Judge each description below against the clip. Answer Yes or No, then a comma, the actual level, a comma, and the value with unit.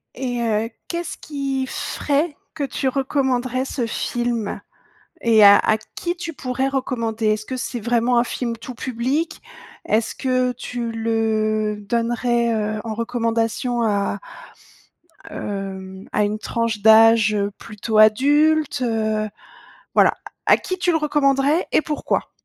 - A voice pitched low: No, high, 235 Hz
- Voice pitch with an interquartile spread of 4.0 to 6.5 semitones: No, average, 3.5 semitones